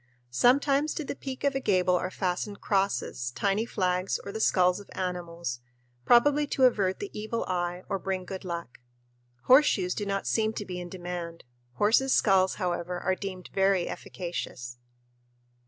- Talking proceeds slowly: No, average, 160 wpm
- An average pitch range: Yes, average, 3.5 semitones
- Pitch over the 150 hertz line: Yes, high, 190 Hz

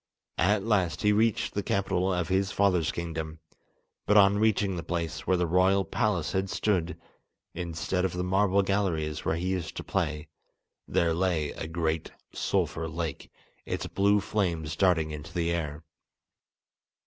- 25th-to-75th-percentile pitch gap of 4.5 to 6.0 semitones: No, average, 3.1 semitones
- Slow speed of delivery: No, average, 155 wpm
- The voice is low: Yes, very low, 90 Hz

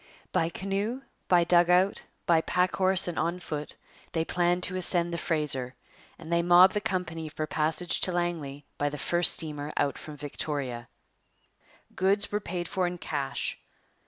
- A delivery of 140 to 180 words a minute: Yes, average, 160 wpm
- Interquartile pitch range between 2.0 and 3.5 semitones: Yes, average, 3.0 semitones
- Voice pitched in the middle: Yes, medium, 170 Hz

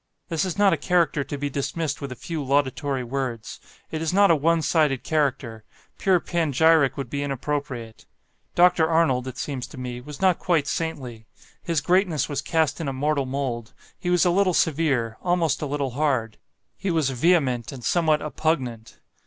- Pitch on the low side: No, medium, 145 Hz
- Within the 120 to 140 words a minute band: No, average, 180 wpm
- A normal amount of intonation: Yes, average, 4.1 semitones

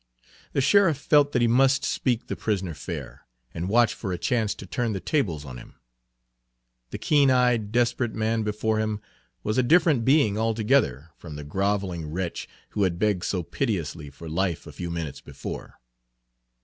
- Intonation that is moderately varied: No, wide, 5.8 semitones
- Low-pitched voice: Yes, low, 105 Hz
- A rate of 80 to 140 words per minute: No, average, 175 wpm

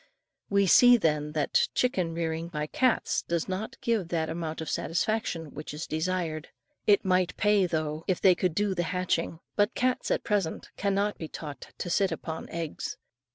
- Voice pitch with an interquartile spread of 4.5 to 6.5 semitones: No, average, 3.8 semitones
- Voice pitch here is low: No, medium, 175 Hz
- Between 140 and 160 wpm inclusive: No, average, 175 wpm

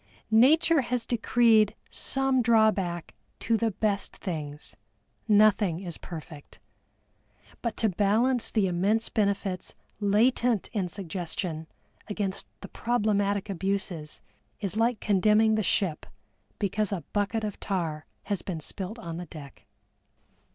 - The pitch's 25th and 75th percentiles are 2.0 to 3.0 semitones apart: No, average, 3.6 semitones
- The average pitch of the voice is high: Yes, high, 205 Hz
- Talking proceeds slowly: Yes, slow, 120 wpm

